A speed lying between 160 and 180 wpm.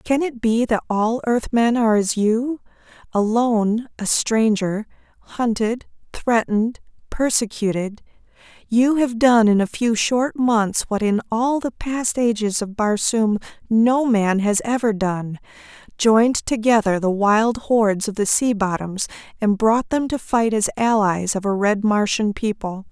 No: average, 150 wpm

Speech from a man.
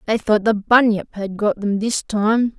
Yes: male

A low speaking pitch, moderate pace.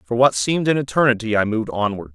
No: low, 115 Hz; fast, 225 wpm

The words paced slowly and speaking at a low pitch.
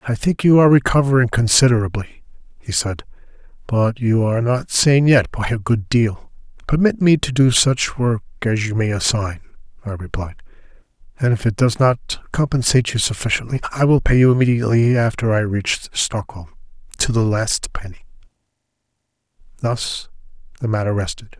No: average, 150 wpm; low, 120 Hz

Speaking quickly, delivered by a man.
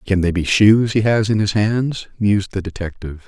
Yes: fast, 220 wpm; male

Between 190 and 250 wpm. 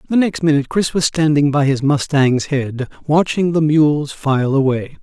No: average, 180 wpm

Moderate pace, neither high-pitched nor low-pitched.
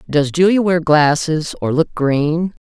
Yes: average, 160 wpm; medium, 160 Hz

